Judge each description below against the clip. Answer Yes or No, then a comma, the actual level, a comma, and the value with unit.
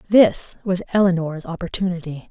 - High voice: No, medium, 175 Hz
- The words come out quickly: No, slow, 105 wpm